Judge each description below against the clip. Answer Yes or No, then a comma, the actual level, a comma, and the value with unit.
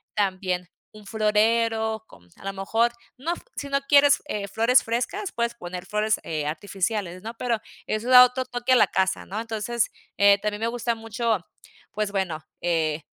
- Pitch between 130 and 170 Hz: No, high, 215 Hz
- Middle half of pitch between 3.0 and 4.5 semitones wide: Yes, average, 3.4 semitones